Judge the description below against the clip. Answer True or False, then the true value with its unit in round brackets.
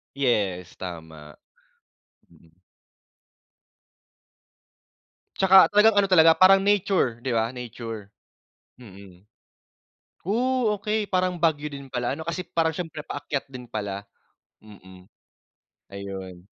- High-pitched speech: False (125 Hz)